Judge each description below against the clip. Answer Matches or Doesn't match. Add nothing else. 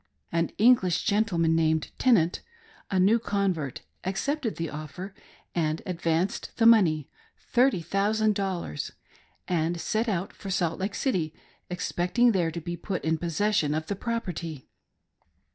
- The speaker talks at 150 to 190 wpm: Doesn't match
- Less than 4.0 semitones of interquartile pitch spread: Doesn't match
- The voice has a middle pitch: Matches